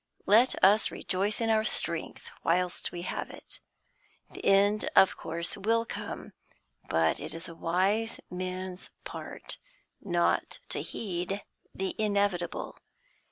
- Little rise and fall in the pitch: No, average, 3.1 semitones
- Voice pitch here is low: No, high, 190 Hz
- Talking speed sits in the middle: No, slow, 125 wpm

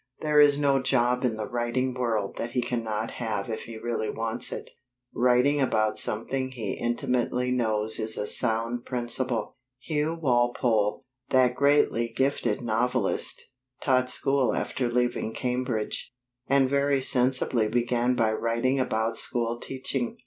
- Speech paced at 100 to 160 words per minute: Yes, average, 140 wpm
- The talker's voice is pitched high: No, low, 120 Hz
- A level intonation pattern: Yes, narrow, 2.3 semitones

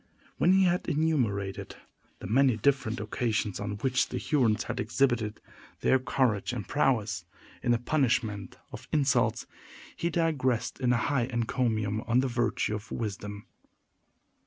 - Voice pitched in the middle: No, low, 120 Hz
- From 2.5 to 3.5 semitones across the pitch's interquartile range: No, average, 4.0 semitones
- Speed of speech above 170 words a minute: No, average, 140 wpm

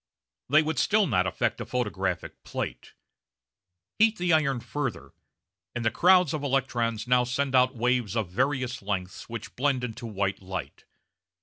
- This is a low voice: Yes, low, 125 Hz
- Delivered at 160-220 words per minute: No, average, 150 wpm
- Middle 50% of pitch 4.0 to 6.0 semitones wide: Yes, average, 5.0 semitones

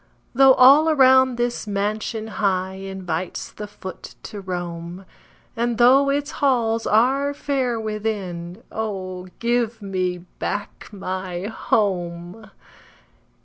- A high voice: Yes, high, 215 Hz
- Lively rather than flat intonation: No, average, 4.5 semitones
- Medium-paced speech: No, slow, 105 wpm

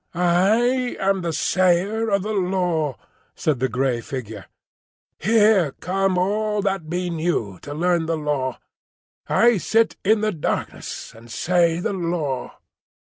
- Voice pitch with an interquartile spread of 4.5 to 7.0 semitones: Yes, average, 4.8 semitones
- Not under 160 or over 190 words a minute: No, slow, 135 wpm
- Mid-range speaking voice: Yes, medium, 175 Hz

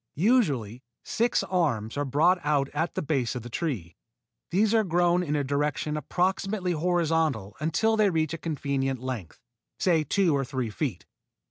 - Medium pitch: Yes, medium, 150 Hz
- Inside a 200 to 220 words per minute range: No, average, 160 wpm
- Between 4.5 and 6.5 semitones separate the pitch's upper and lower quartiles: Yes, average, 4.9 semitones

